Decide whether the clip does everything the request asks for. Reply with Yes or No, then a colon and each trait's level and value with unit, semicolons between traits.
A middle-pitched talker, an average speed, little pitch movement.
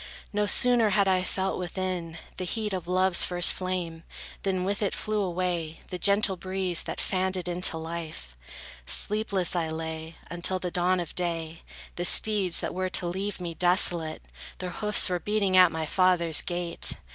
Yes: medium, 180 Hz; average, 170 wpm; narrow, 2.0 semitones